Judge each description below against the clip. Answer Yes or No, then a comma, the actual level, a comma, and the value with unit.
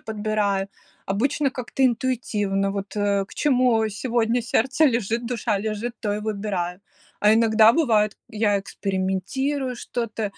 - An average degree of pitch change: Yes, average, 3.3 semitones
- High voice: Yes, high, 220 Hz